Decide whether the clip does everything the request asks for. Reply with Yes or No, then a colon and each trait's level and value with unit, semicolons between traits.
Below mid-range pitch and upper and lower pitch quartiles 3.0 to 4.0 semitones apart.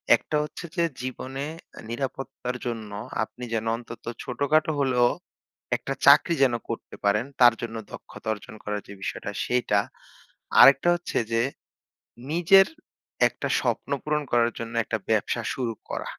Yes: low, 125 Hz; average, 3.5 semitones